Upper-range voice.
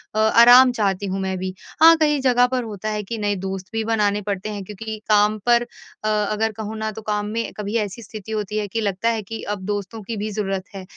Yes: high, 215 Hz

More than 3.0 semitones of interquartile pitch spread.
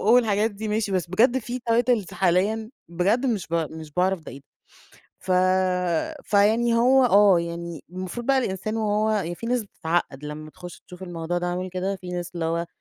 Yes: average, 4.2 semitones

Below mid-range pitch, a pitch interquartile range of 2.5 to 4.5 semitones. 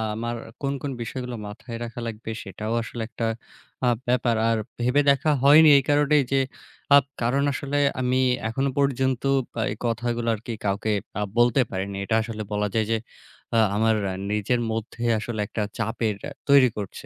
Yes: low, 120 Hz; average, 3.2 semitones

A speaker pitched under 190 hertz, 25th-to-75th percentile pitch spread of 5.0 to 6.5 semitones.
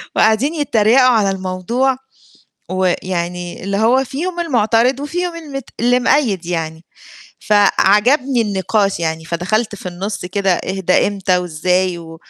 No: high, 205 Hz; wide, 5.5 semitones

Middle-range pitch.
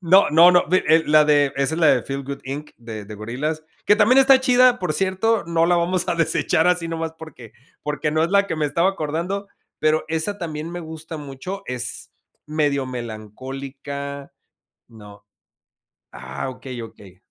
Yes: medium, 155 Hz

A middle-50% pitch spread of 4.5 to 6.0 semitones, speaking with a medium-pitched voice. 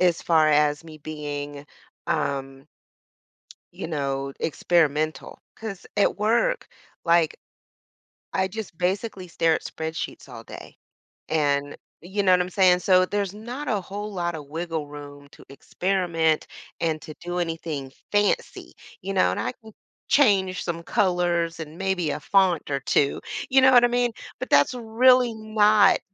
Yes: average, 4.9 semitones; medium, 175 Hz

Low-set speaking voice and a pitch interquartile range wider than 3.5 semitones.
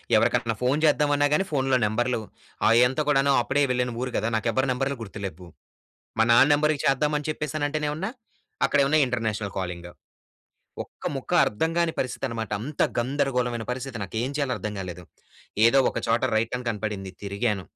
Yes: low, 125 Hz; average, 4.5 semitones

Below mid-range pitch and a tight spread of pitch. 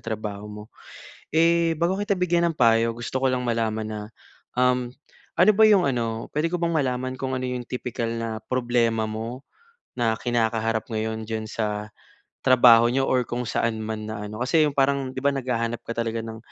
No: low, 120 Hz; average, 3.0 semitones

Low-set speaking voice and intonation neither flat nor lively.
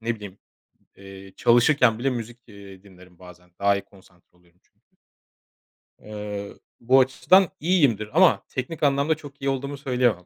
No: low, 115 Hz; wide, 5.7 semitones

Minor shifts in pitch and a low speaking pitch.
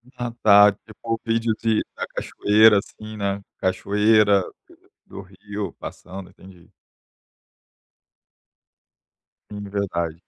Yes: narrow, 2.0 semitones; low, 105 Hz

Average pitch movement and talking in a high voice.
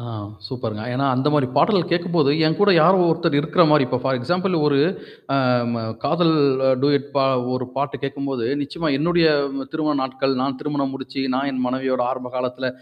No: average, 3.5 semitones; medium, 140 Hz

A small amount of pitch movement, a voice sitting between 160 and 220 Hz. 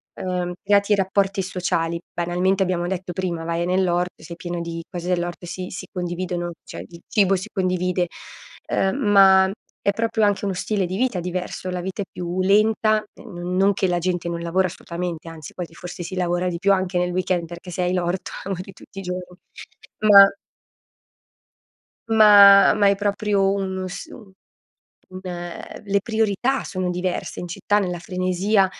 Yes: narrow, 2.0 semitones; medium, 185 Hz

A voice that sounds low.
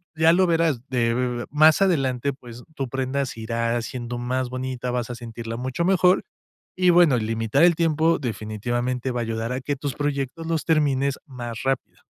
Yes: low, 130 Hz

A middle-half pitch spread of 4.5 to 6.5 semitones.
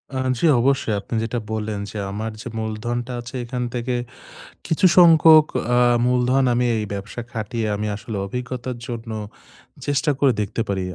No: average, 2.8 semitones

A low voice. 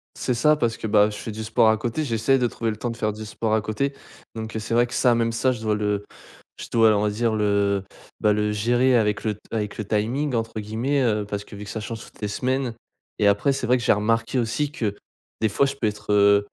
Yes: low, 110 Hz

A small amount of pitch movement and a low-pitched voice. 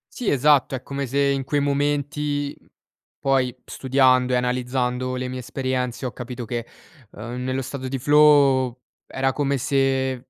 Yes: narrow, 1.8 semitones; low, 130 Hz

